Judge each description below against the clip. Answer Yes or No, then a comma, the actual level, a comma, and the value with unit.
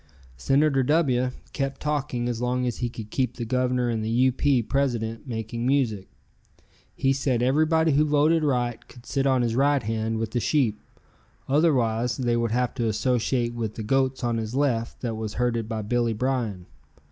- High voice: No, low, 125 Hz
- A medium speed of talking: Yes, average, 180 wpm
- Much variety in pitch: No, average, 3.0 semitones